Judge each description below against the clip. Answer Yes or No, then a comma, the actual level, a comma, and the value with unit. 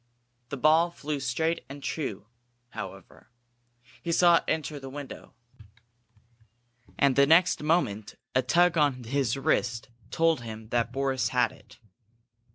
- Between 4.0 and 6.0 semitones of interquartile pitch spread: Yes, average, 4.4 semitones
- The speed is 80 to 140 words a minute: Yes, slow, 135 wpm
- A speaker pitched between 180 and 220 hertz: No, medium, 140 Hz